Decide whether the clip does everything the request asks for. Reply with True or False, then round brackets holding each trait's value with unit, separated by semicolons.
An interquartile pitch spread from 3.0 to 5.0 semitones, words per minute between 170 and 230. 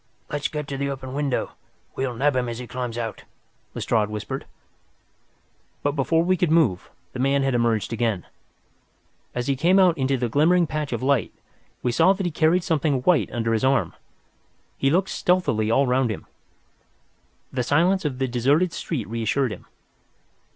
True (4.7 semitones; 180 wpm)